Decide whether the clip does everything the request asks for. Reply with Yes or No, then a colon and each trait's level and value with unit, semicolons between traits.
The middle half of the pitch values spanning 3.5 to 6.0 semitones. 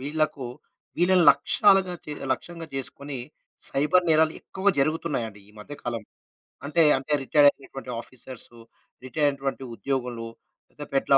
Yes: average, 3.9 semitones